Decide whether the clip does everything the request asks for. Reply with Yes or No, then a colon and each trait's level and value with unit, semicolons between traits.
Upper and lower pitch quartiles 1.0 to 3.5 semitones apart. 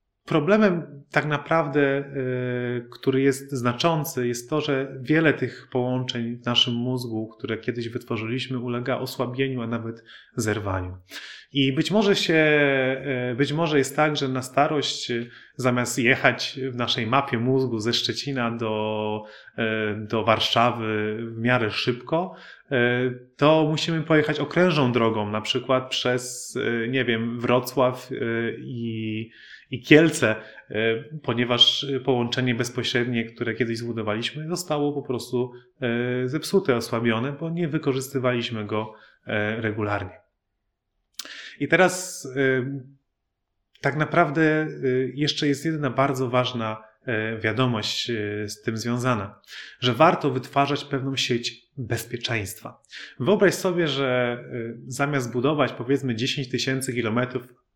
Yes: average, 3.2 semitones